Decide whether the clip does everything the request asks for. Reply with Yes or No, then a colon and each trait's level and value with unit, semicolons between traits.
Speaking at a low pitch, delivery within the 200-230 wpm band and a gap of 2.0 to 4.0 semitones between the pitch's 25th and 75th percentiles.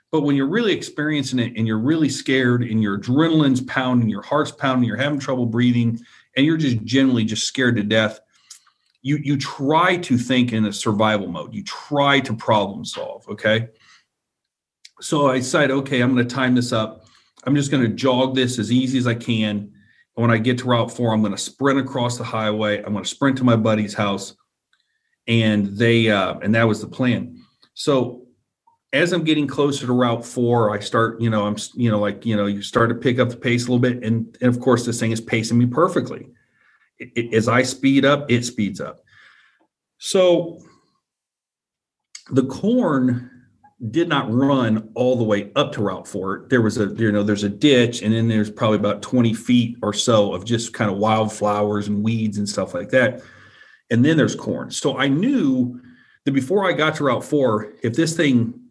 Yes: low, 120 Hz; fast, 205 wpm; average, 3.6 semitones